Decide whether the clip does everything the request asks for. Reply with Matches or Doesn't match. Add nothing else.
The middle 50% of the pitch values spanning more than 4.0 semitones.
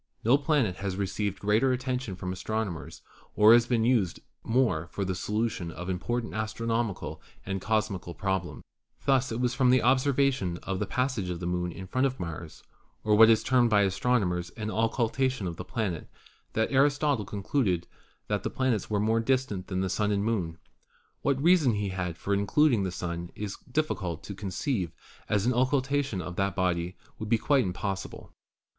Matches